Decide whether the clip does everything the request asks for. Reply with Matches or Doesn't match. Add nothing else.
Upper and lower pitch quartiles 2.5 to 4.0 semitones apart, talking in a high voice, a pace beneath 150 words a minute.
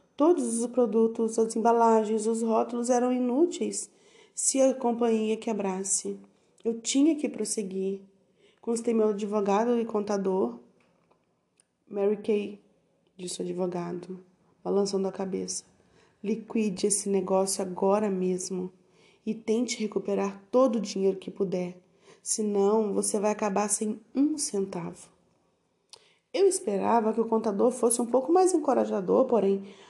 Matches